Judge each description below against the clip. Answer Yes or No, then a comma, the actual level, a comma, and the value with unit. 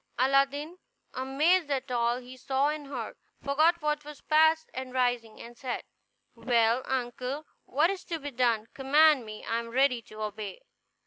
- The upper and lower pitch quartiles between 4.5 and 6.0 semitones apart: No, average, 3.7 semitones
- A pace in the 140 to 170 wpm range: Yes, average, 155 wpm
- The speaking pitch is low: No, very high, 265 Hz